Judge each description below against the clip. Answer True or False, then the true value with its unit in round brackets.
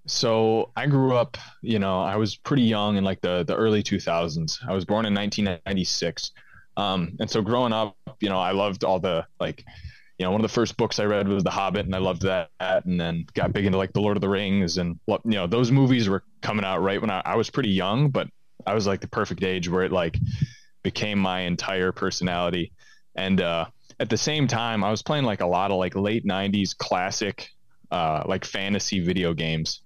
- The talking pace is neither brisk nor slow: False (225 wpm)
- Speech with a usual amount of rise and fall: True (3.0 semitones)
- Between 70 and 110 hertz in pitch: True (100 Hz)